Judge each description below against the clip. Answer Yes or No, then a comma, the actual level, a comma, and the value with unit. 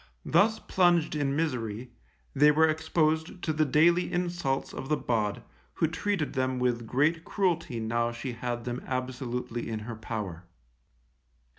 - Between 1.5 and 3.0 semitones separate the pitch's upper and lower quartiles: No, average, 5.1 semitones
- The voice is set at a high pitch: No, low, 135 Hz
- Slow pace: No, average, 145 wpm